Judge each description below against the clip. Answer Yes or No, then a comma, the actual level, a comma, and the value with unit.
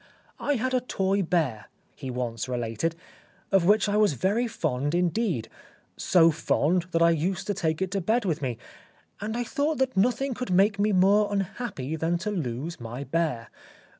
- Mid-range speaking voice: Yes, medium, 180 Hz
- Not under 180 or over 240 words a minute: Yes, average, 190 wpm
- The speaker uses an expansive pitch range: Yes, wide, 5.9 semitones